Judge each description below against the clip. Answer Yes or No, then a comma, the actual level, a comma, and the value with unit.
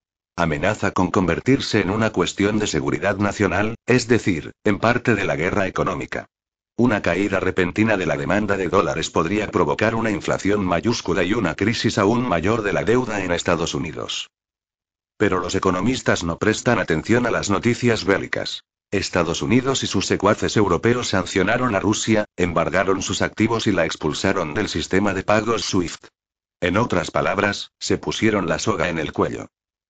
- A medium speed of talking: Yes, average, 165 wpm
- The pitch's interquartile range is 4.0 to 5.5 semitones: No, average, 3.2 semitones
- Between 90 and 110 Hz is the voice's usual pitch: Yes, low, 100 Hz